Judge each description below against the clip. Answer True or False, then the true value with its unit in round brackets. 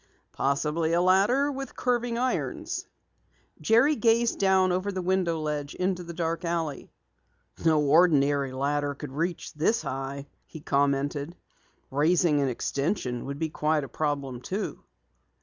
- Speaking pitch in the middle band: True (160 Hz)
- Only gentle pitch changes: False (4.8 semitones)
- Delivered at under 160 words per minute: True (135 wpm)